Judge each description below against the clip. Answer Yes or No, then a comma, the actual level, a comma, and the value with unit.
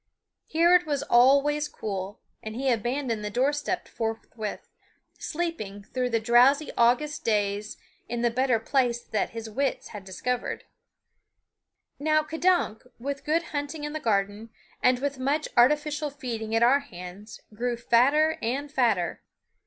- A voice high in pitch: Yes, very high, 250 Hz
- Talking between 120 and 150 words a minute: Yes, average, 145 wpm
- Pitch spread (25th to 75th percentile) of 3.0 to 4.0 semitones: No, average, 4.7 semitones